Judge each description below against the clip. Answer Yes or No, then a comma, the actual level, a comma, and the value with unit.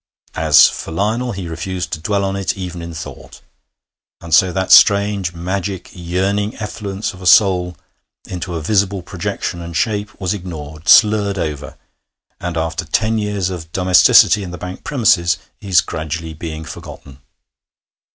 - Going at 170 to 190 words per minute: No, average, 150 wpm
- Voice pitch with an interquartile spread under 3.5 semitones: Yes, average, 3.1 semitones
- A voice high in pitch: No, very low, 90 Hz